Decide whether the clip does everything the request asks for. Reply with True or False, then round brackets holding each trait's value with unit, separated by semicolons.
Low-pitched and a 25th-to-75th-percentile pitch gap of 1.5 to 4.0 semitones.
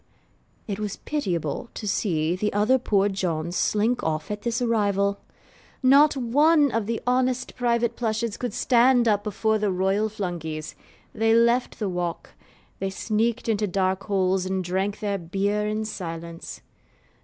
False (210 Hz; 3.7 semitones)